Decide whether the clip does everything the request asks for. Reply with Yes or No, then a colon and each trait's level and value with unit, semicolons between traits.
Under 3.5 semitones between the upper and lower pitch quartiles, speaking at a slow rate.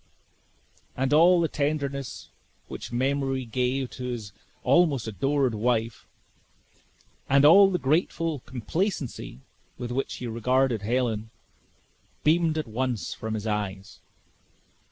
No: average, 4.4 semitones; slow, 115 wpm